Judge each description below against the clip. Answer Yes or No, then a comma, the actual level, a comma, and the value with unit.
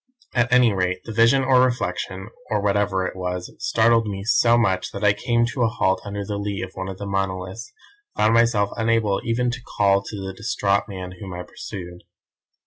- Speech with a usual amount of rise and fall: Yes, average, 3.4 semitones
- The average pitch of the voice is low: Yes, low, 100 Hz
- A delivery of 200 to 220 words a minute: Yes, fast, 205 wpm